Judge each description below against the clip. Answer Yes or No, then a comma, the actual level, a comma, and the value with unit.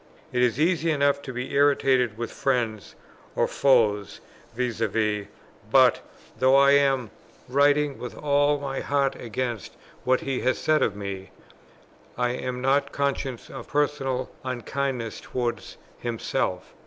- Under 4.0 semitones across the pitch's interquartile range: Yes, average, 3.0 semitones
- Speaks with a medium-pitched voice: No, low, 130 Hz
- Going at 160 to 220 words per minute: No, average, 140 wpm